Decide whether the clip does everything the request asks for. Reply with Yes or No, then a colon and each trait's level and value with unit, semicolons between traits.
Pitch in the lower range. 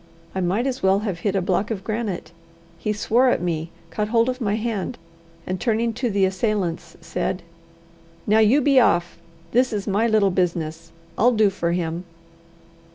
No: high, 205 Hz